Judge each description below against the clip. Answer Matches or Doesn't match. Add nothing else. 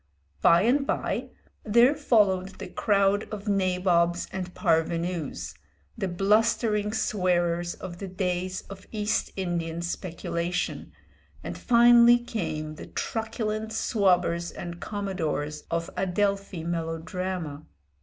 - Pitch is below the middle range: Doesn't match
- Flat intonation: Doesn't match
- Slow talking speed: Matches